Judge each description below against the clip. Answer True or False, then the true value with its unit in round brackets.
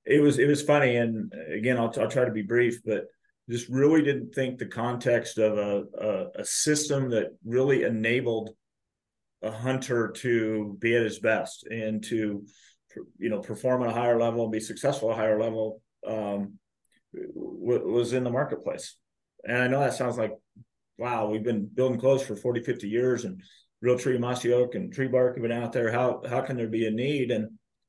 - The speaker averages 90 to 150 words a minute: False (195 wpm)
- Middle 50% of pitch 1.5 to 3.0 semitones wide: True (2.7 semitones)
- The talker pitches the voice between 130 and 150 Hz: False (120 Hz)